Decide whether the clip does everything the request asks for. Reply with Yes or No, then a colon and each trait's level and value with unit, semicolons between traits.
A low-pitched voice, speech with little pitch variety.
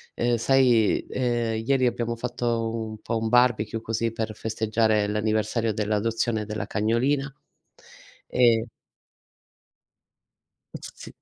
Yes: low, 115 Hz; narrow, 1.7 semitones